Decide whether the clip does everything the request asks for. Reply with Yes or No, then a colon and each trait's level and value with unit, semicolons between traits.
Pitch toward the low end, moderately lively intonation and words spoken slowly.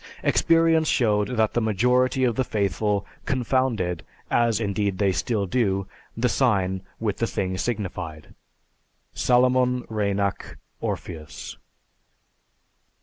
Yes: low, 110 Hz; average, 4.2 semitones; slow, 105 wpm